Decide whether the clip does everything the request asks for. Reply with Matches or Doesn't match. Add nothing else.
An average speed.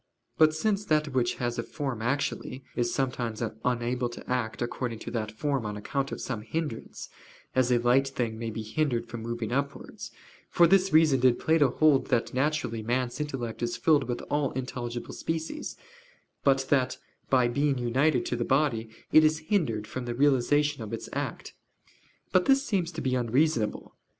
Matches